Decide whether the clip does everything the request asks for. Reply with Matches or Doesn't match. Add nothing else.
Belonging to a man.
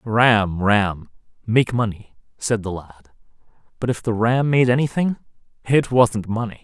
Matches